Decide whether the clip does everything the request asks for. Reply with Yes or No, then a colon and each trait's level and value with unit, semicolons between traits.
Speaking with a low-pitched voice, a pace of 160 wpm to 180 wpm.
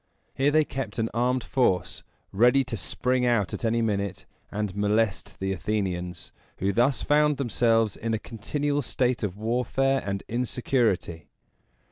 No: low, 115 Hz; average, 145 wpm